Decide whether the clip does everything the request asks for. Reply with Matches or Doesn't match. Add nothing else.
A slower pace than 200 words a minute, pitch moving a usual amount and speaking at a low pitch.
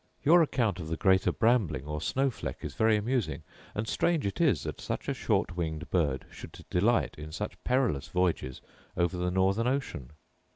Doesn't match